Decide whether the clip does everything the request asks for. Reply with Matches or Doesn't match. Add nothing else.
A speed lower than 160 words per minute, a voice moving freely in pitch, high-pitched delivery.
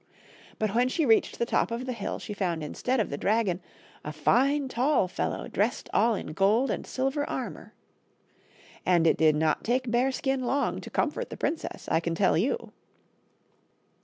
Doesn't match